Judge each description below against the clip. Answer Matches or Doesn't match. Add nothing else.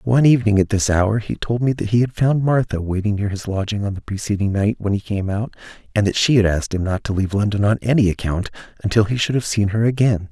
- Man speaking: Matches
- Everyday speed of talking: Doesn't match